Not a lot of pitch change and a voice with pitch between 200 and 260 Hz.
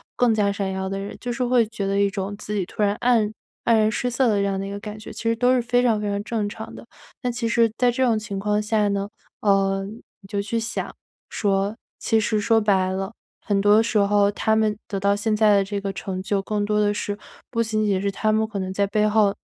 Yes: narrow, 1.9 semitones; high, 210 Hz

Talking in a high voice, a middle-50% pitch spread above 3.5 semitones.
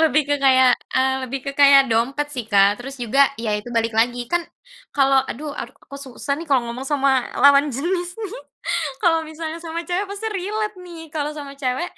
Yes: very high, 280 Hz; average, 4.0 semitones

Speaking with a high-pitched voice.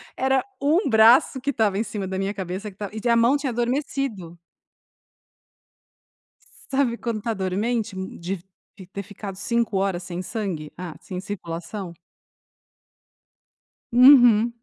Yes: high, 215 Hz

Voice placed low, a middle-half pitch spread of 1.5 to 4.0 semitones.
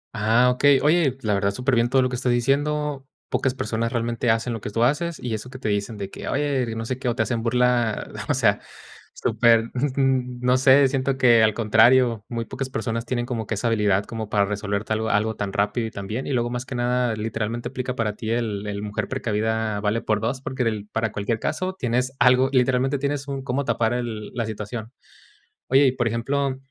Yes: low, 120 Hz; average, 2.9 semitones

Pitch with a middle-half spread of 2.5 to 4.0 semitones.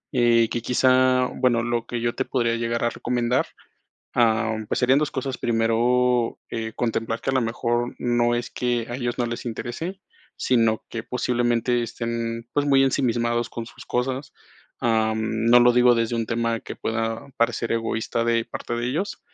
No: narrow, 1.2 semitones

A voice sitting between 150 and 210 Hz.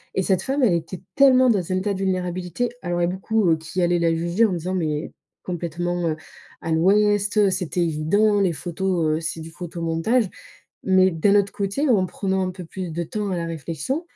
Yes: medium, 185 Hz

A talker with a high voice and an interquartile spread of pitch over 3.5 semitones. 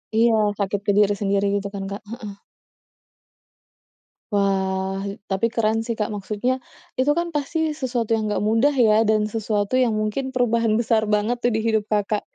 No: high, 220 Hz; average, 2.8 semitones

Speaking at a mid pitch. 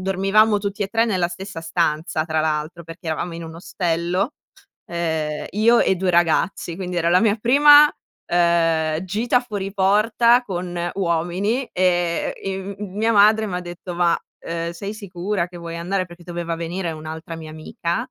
Yes: medium, 175 Hz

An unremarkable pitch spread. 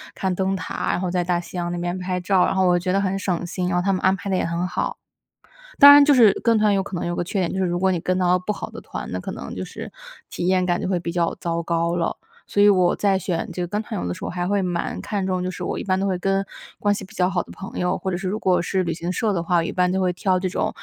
No: narrow, 1.6 semitones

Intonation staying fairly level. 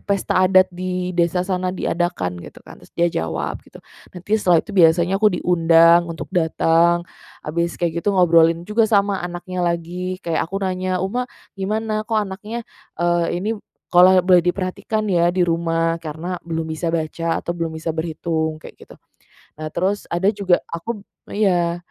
Yes: narrow, 2.1 semitones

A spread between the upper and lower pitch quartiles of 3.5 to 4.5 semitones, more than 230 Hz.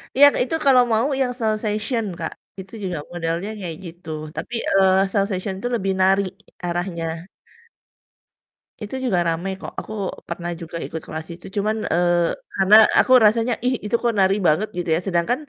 No: average, 3.9 semitones; high, 190 Hz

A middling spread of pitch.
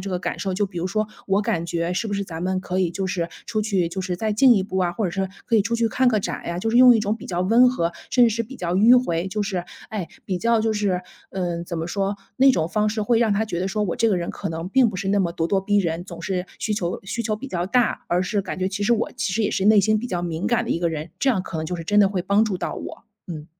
Yes: average, 3.5 semitones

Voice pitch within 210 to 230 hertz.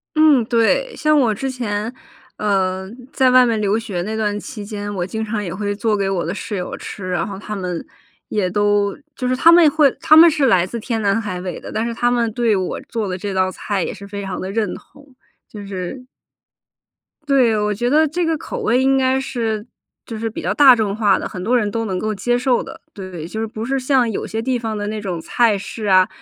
Yes: high, 215 Hz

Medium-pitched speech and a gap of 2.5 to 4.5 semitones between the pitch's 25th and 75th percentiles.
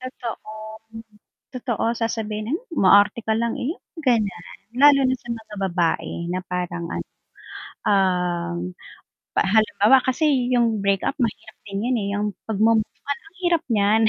No: high, 220 Hz; average, 3.8 semitones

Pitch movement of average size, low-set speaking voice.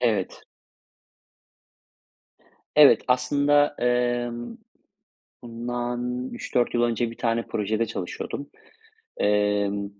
No: narrow, 2.1 semitones; low, 120 Hz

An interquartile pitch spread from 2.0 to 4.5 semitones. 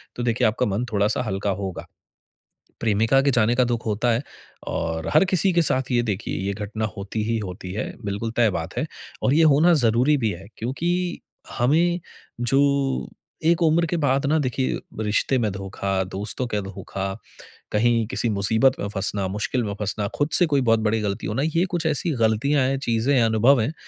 No: average, 4.9 semitones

